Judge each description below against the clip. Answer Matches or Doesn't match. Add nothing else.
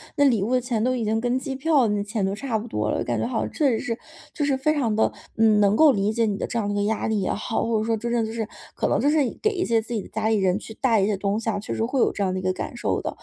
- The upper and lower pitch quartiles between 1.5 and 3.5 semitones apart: Matches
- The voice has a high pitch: Matches